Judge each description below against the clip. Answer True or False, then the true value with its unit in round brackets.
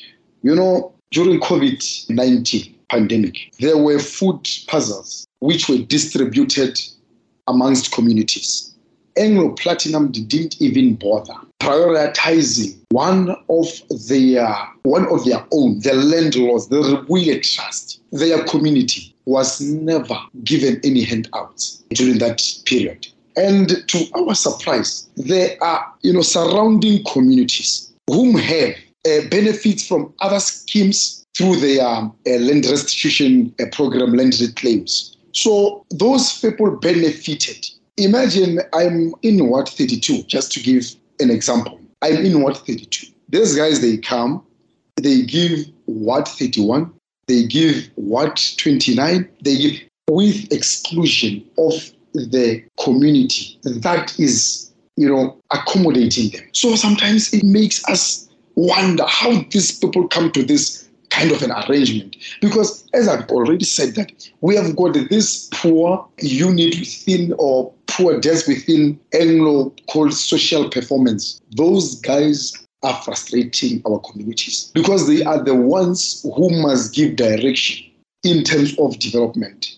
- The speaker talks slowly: True (125 wpm)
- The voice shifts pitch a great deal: True (6.9 semitones)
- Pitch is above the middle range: False (155 Hz)